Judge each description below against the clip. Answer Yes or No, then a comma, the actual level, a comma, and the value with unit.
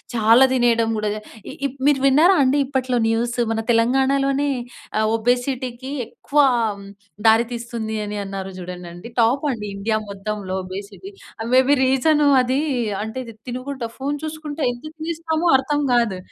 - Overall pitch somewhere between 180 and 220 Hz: No, high, 245 Hz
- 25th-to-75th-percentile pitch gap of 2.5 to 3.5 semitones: No, average, 3.9 semitones